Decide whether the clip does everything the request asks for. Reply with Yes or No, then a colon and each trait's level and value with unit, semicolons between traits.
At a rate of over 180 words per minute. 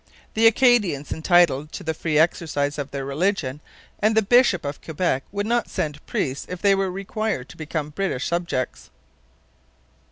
No: average, 165 wpm